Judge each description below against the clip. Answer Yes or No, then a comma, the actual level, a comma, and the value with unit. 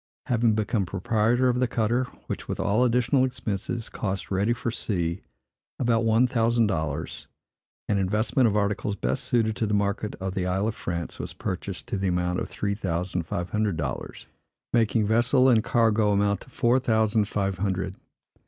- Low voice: Yes, low, 105 Hz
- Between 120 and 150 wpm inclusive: No, average, 175 wpm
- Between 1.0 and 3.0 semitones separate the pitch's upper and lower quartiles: No, average, 3.4 semitones